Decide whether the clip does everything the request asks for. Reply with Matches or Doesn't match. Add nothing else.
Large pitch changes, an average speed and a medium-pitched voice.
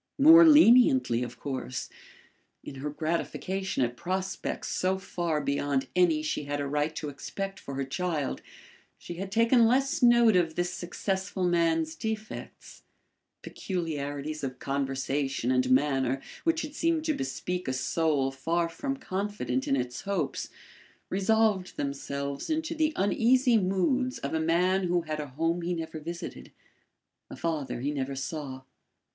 Matches